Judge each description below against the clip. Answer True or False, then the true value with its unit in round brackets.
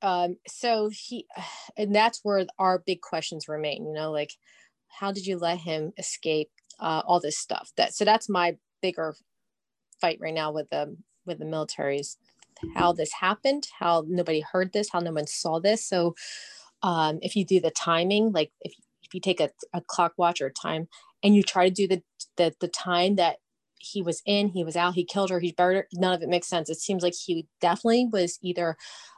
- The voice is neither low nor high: True (180 Hz)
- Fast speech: True (210 wpm)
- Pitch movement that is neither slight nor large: True (3.2 semitones)